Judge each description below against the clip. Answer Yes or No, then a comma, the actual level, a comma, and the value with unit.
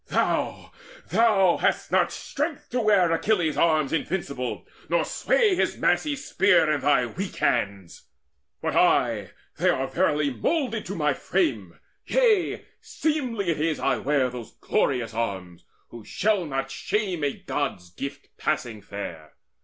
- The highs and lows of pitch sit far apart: Yes, wide, 8.9 semitones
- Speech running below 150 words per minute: Yes, average, 140 wpm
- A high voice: No, medium, 155 Hz